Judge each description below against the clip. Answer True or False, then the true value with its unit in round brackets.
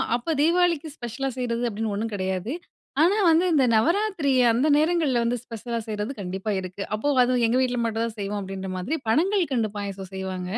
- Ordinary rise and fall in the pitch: False (6.4 semitones)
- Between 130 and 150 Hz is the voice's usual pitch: False (235 Hz)